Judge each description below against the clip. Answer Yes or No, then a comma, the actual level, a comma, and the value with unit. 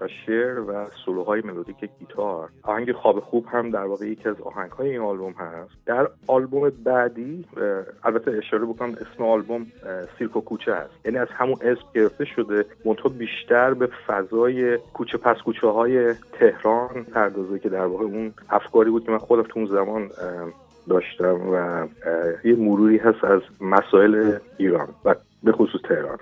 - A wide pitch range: No, average, 2.7 semitones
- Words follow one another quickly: Yes, fast, 160 wpm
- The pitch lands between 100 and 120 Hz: Yes, low, 110 Hz